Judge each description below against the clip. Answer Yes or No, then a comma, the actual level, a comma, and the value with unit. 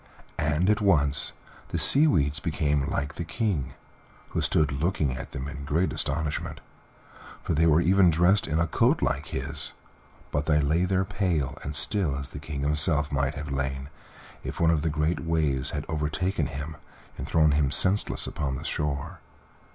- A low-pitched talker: Yes, very low, 75 Hz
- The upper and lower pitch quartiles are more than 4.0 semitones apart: No, average, 2.8 semitones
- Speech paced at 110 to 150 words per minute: No, average, 175 wpm